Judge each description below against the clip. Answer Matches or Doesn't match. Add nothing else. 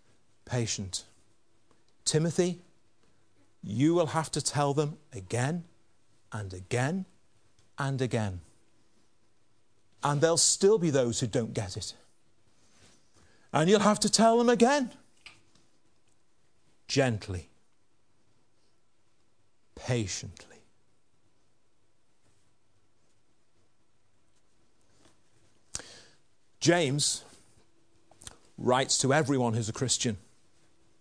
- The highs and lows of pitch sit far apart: Doesn't match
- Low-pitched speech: Matches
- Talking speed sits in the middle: Doesn't match